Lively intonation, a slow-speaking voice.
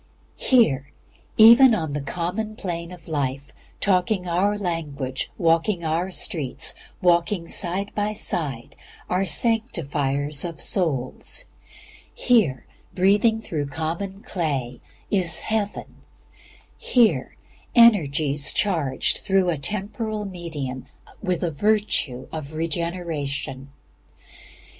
Yes: wide, 5.8 semitones; slow, 100 wpm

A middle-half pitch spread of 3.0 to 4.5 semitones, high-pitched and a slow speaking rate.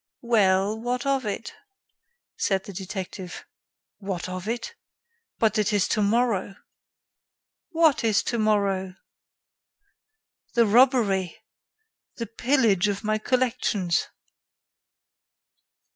Yes: average, 3.6 semitones; high, 210 Hz; slow, 90 wpm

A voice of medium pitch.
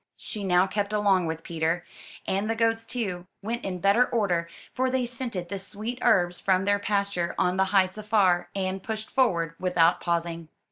No: high, 195 Hz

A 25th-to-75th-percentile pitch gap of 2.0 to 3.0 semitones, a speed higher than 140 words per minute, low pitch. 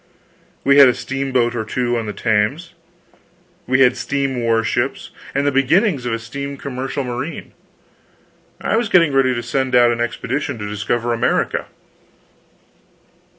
Yes: average, 2.7 semitones; average, 150 wpm; low, 130 Hz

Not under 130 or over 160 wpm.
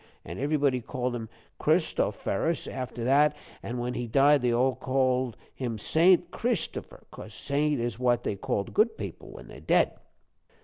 Yes: average, 150 wpm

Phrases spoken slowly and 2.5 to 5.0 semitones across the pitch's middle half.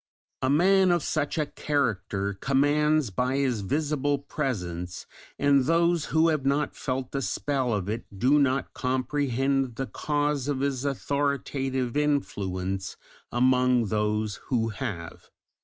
Yes: slow, 130 wpm; average, 3.8 semitones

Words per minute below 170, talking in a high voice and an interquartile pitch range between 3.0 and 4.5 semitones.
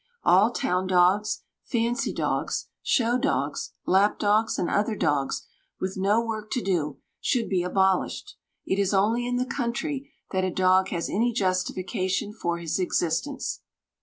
Yes: average, 150 wpm; high, 195 Hz; average, 4.0 semitones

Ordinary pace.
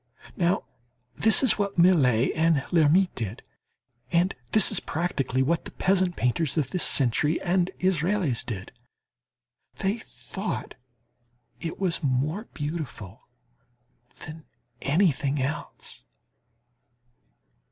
No: slow, 105 wpm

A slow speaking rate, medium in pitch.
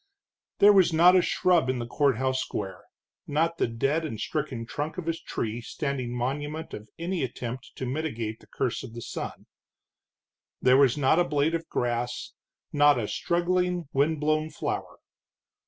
No: average, 160 wpm; medium, 145 Hz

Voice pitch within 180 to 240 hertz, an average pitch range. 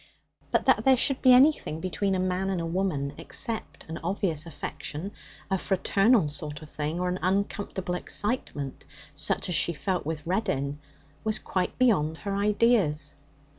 Yes: medium, 185 Hz; average, 4.7 semitones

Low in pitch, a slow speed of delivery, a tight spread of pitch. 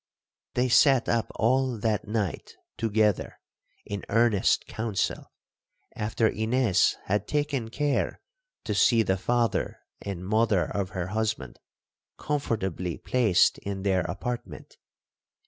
No: low, 110 Hz; slow, 110 wpm; average, 3.3 semitones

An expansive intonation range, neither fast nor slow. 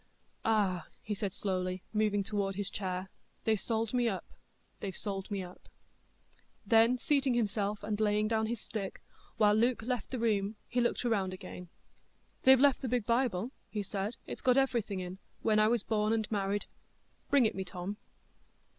No: average, 2.9 semitones; average, 165 wpm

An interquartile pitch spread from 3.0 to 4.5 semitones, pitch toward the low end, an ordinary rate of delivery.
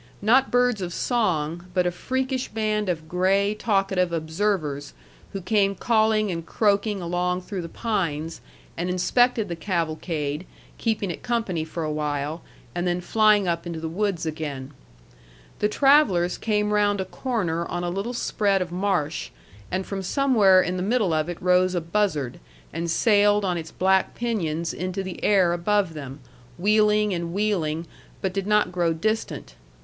No: average, 3.9 semitones; medium, 185 Hz; average, 165 wpm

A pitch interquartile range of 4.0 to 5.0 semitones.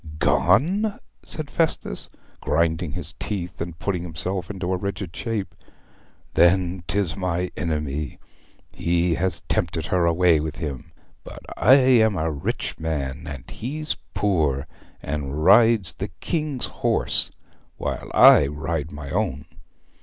Yes: average, 4.7 semitones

